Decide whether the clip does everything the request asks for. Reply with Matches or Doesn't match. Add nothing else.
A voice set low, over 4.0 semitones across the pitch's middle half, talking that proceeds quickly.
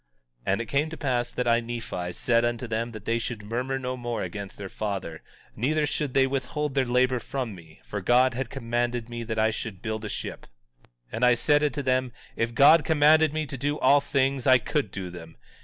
Doesn't match